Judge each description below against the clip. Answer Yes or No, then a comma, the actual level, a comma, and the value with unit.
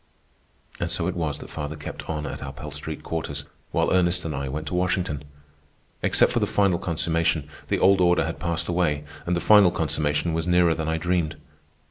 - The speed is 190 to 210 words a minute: Yes, average, 200 wpm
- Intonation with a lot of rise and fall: No, average, 2.8 semitones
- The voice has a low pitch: Yes, very low, 80 Hz